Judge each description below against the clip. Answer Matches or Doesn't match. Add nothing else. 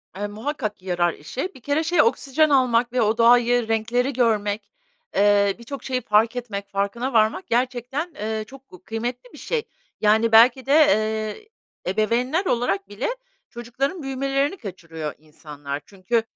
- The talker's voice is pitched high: Matches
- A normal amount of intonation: Matches